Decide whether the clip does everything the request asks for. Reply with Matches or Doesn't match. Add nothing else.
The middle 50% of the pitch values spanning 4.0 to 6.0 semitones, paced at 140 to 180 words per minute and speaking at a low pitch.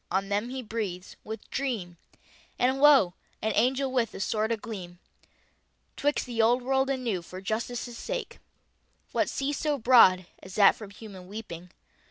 Doesn't match